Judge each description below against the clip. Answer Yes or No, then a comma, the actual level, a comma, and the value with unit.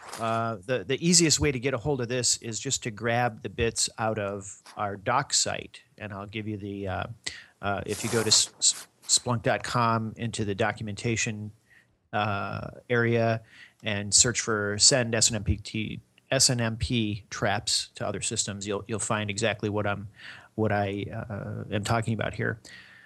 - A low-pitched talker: Yes, low, 110 Hz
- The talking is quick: No, average, 165 wpm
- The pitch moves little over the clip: Yes, narrow, 2.3 semitones